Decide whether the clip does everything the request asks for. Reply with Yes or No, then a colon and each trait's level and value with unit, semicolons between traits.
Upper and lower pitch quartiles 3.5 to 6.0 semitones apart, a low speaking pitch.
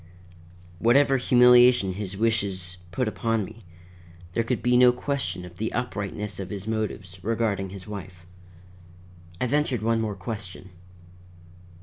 Yes: average, 4.2 semitones; low, 110 Hz